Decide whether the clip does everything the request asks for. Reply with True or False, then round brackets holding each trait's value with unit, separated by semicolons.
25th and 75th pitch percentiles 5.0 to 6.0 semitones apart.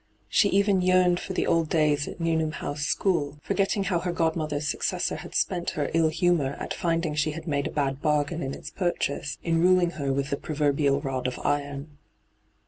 False (3.3 semitones)